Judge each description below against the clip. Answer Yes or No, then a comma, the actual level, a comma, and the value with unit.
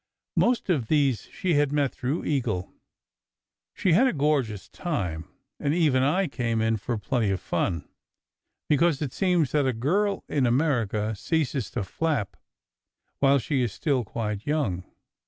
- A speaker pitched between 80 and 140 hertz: Yes, low, 135 Hz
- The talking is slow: No, average, 155 wpm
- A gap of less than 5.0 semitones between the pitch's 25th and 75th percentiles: No, wide, 5.5 semitones